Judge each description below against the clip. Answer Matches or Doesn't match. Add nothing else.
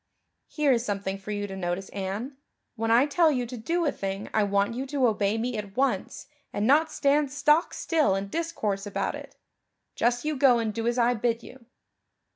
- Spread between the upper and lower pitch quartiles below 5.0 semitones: Doesn't match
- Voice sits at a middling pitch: Doesn't match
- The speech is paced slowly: Doesn't match